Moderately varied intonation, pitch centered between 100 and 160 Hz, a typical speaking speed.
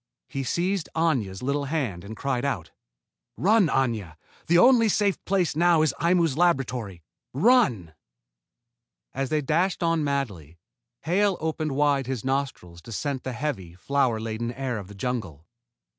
No: wide, 6.8 semitones; low, 135 Hz; average, 145 wpm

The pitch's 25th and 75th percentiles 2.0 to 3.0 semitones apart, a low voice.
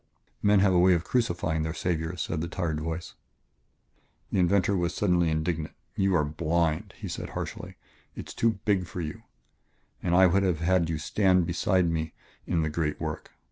Yes: narrow, 2.5 semitones; very low, 85 Hz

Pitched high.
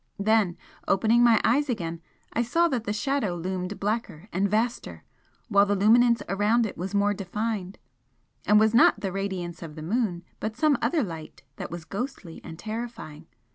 Yes: high, 205 Hz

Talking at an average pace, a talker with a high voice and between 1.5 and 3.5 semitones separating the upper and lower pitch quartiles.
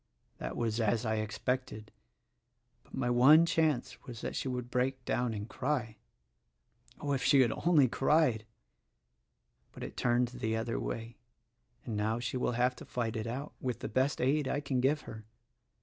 No: average, 175 wpm; low, 125 Hz; average, 2.9 semitones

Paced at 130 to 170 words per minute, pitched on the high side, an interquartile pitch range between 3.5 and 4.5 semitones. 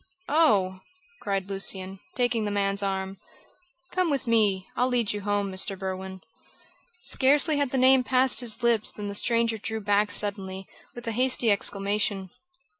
Yes: average, 155 wpm; high, 205 Hz; average, 3.9 semitones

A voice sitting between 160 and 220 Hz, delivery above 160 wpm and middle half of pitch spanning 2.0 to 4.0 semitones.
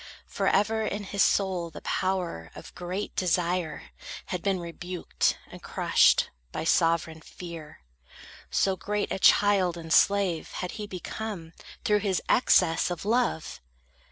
No: medium, 185 Hz; slow, 135 wpm; average, 3.2 semitones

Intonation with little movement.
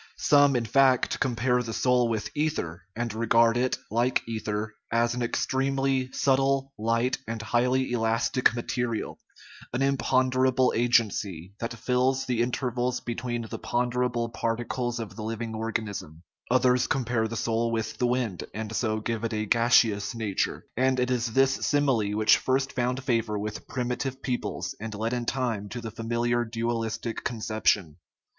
Yes: narrow, 2.2 semitones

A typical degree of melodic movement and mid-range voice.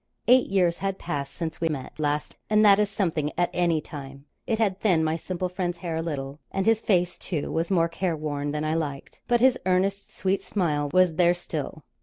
Yes: average, 3.9 semitones; medium, 175 Hz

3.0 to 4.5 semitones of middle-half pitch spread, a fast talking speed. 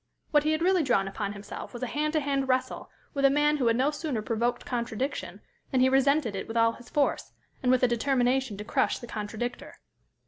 Yes: average, 3.5 semitones; fast, 220 wpm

